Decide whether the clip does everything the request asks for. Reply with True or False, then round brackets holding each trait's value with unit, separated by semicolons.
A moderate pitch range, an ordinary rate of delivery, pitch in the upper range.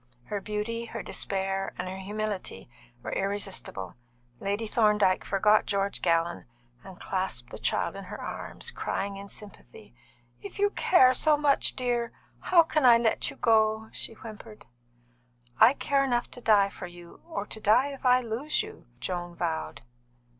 True (3.9 semitones; 160 wpm; 210 Hz)